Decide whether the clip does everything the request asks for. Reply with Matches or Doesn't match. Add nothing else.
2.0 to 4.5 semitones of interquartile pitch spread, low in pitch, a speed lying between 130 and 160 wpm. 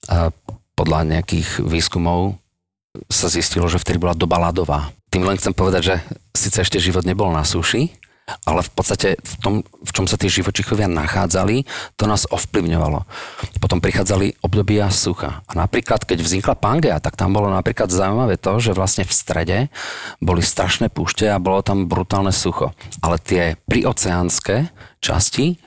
Matches